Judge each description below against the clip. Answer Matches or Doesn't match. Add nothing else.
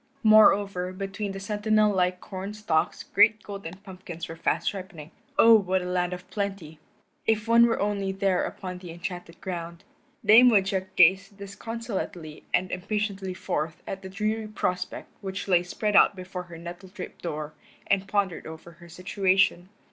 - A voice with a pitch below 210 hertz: Matches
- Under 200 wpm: Matches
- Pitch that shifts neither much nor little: Doesn't match